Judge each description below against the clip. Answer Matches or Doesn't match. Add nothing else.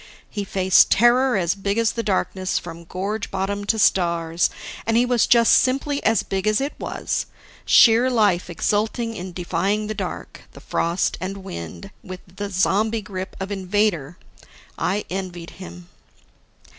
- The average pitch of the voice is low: Doesn't match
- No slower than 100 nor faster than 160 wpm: Matches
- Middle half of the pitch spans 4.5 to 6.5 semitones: Doesn't match